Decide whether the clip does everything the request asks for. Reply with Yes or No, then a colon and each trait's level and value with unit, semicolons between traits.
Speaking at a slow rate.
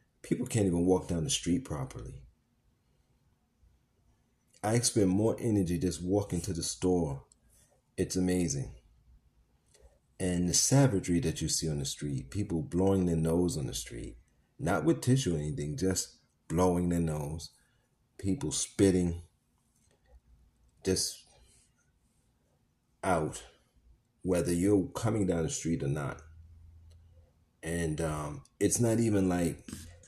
Yes: slow, 125 wpm